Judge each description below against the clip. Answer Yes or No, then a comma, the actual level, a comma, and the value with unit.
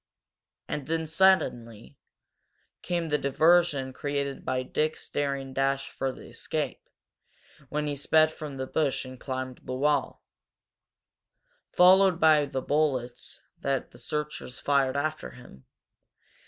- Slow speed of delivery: Yes, slow, 125 wpm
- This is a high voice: No, medium, 140 Hz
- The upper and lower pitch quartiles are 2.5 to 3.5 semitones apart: Yes, average, 2.9 semitones